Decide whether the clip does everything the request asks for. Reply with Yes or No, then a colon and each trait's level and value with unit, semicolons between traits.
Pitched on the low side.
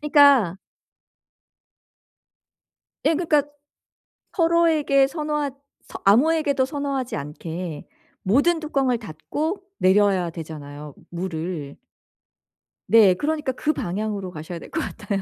No: high, 230 Hz